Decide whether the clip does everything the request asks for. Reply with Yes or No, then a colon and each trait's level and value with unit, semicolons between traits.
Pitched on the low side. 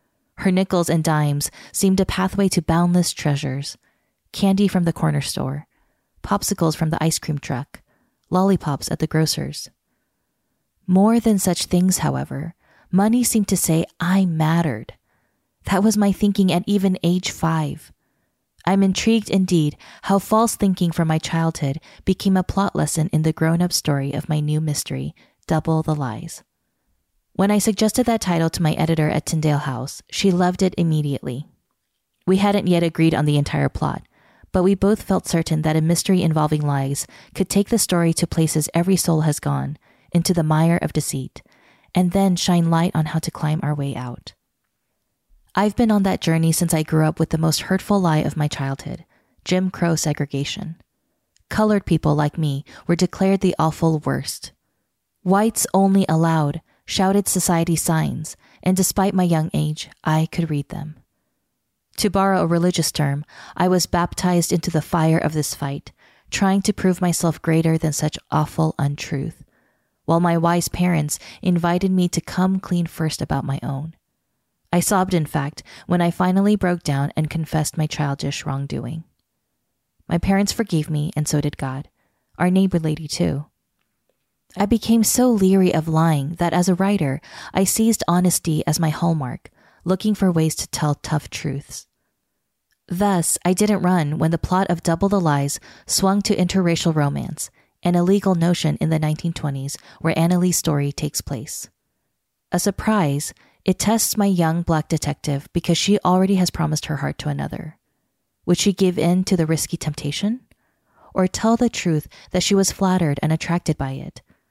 No: medium, 165 Hz